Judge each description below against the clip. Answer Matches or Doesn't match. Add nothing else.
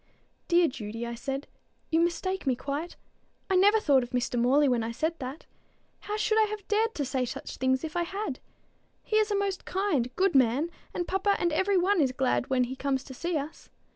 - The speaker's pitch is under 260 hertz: Doesn't match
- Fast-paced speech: Matches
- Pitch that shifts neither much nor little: Doesn't match